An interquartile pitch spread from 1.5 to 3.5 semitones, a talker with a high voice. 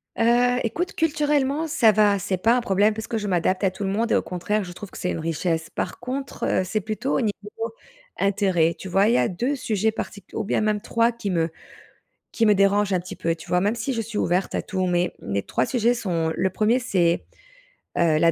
No: average, 4.1 semitones; high, 205 Hz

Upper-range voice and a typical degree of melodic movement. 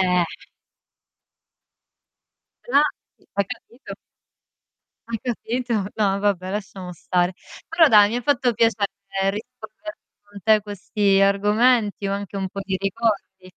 Yes: high, 205 Hz; average, 3.1 semitones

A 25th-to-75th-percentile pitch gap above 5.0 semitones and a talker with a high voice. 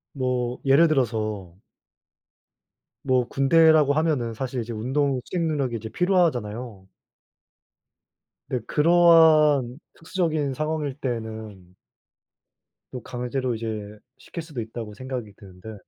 No: wide, 5.4 semitones; low, 130 Hz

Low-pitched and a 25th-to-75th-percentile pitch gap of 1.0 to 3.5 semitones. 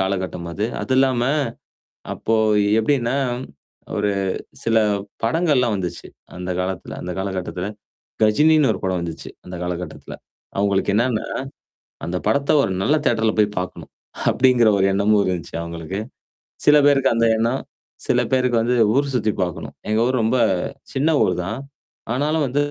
No: low, 110 Hz; wide, 5.6 semitones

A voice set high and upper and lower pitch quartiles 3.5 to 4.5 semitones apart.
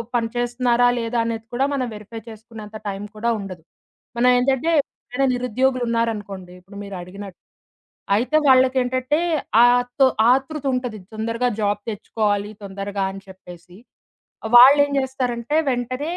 Yes: high, 235 Hz; average, 3.8 semitones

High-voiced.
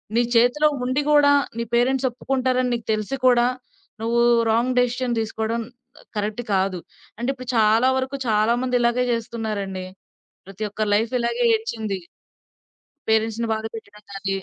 Yes: high, 235 Hz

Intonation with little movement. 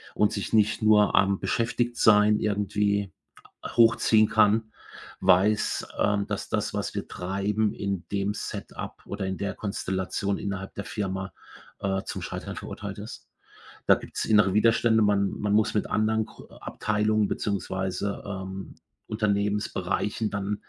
Yes: narrow, 1.5 semitones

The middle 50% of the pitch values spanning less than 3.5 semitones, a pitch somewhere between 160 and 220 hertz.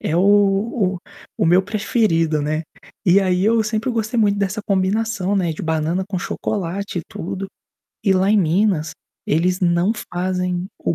Yes: average, 2.8 semitones; high, 190 Hz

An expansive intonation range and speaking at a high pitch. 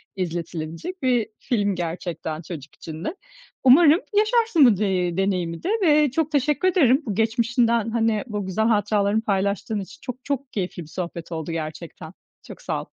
Yes: wide, 6.8 semitones; high, 210 Hz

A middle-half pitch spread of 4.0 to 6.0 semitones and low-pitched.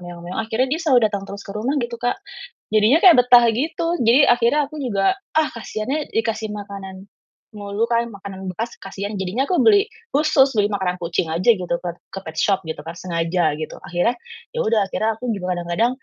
No: average, 4.6 semitones; high, 215 Hz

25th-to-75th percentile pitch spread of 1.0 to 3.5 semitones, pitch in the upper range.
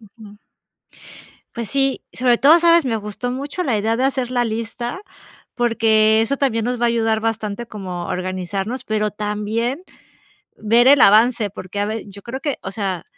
Yes: average, 3.1 semitones; high, 225 Hz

